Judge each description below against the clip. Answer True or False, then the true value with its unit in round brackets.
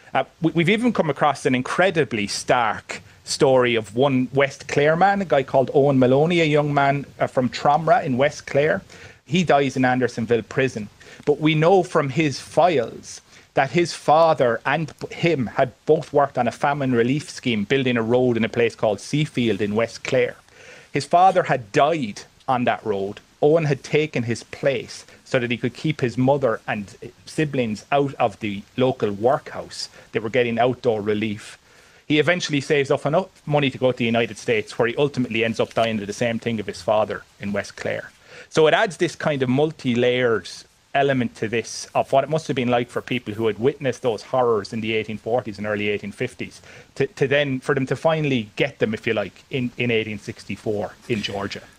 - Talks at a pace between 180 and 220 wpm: True (195 wpm)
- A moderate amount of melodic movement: True (4.2 semitones)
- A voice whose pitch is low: True (130 Hz)